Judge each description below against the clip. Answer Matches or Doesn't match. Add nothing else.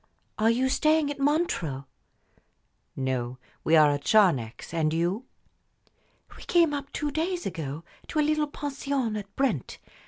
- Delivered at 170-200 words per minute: Doesn't match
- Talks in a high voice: Matches